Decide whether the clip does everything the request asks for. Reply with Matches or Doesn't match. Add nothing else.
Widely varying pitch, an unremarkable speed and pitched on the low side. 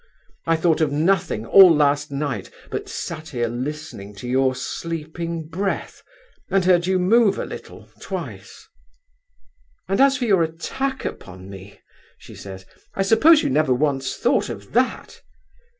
Doesn't match